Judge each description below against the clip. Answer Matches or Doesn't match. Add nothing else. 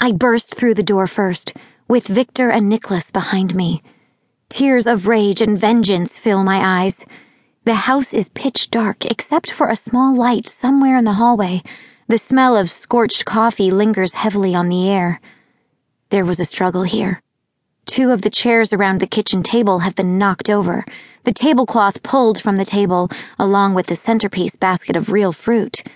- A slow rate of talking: Doesn't match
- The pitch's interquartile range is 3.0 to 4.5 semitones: Matches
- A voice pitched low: Doesn't match